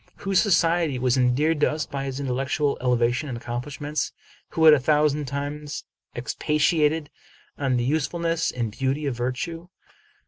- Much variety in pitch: No, average, 3.4 semitones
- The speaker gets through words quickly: No, average, 160 wpm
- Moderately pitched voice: Yes, medium, 145 Hz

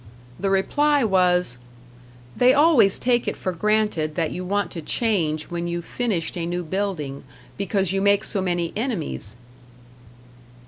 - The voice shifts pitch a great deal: No, average, 3.8 semitones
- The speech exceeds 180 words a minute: No, average, 145 wpm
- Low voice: No, high, 190 Hz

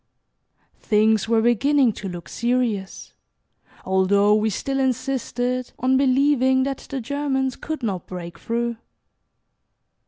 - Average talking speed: No, slow, 115 wpm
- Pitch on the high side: Yes, high, 245 Hz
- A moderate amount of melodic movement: Yes, average, 4.0 semitones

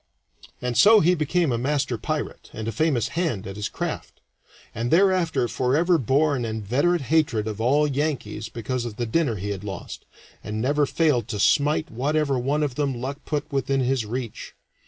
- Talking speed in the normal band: Yes, average, 180 wpm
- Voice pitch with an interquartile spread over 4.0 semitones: Yes, average, 4.9 semitones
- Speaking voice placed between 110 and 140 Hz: Yes, low, 135 Hz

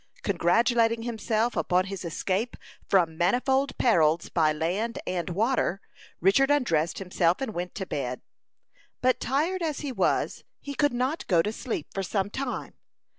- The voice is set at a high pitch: Yes, high, 210 Hz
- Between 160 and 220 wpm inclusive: No, average, 150 wpm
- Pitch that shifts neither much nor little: No, wide, 6.5 semitones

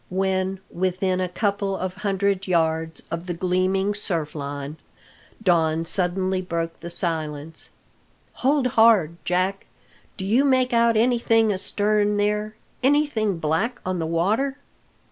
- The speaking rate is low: Yes, slow, 125 wpm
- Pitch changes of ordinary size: Yes, average, 4.0 semitones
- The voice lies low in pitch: No, high, 190 Hz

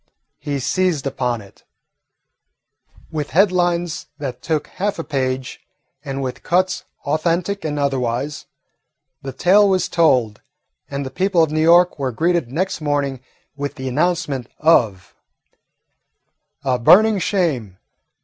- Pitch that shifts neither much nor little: Yes, average, 5.0 semitones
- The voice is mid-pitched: Yes, medium, 150 Hz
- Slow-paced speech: Yes, slow, 125 wpm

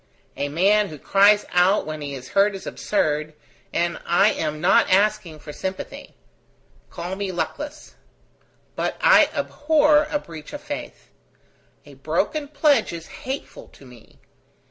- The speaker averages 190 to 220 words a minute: No, average, 145 wpm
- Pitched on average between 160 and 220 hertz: Yes, high, 190 Hz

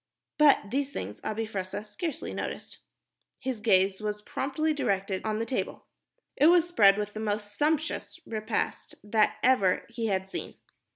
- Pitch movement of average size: Yes, average, 4.7 semitones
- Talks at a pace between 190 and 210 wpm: No, average, 155 wpm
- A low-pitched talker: No, high, 215 Hz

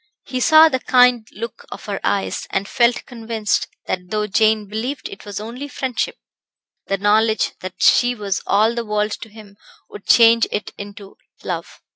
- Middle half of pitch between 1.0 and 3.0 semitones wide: Yes, average, 2.7 semitones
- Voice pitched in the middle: No, high, 220 Hz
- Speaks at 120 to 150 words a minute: No, average, 170 wpm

